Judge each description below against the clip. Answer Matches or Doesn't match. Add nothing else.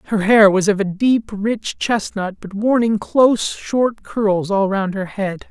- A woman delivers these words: Doesn't match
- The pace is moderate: Matches